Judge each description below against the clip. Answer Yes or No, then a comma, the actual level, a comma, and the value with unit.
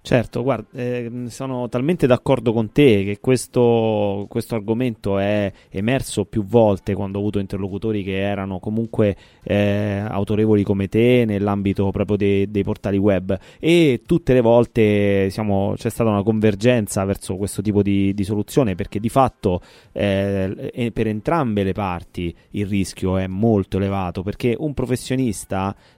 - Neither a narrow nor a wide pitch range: Yes, average, 3.2 semitones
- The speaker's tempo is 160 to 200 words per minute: No, average, 150 wpm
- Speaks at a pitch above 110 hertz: No, low, 105 Hz